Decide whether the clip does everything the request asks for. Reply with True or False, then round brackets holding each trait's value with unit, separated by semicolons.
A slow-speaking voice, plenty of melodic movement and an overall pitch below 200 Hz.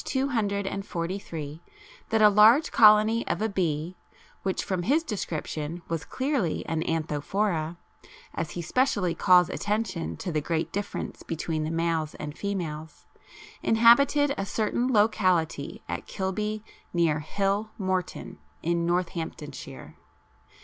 False (120 wpm; 4.6 semitones; 185 Hz)